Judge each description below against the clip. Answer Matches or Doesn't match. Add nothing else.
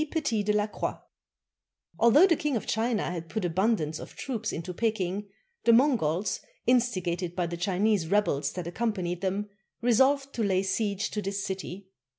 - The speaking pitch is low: Doesn't match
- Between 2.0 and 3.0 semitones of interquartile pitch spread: Doesn't match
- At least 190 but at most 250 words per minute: Doesn't match